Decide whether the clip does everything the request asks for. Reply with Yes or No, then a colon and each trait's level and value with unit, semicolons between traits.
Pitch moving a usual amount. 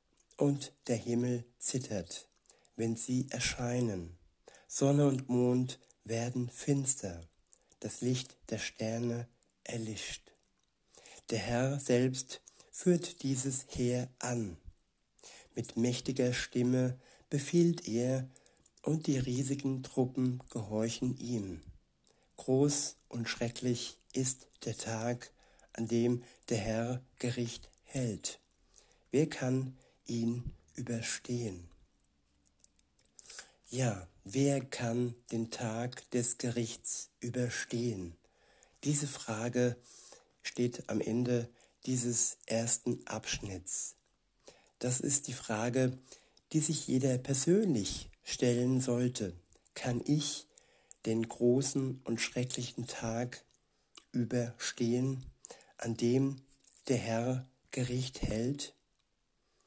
No: narrow, 2.1 semitones